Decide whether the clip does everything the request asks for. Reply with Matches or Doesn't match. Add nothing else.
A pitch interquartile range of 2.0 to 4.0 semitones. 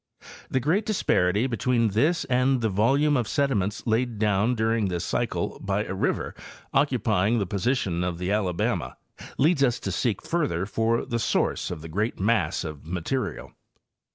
Doesn't match